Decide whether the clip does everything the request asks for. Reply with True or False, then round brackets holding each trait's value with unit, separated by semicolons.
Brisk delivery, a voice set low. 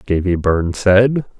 False (130 wpm; 100 Hz)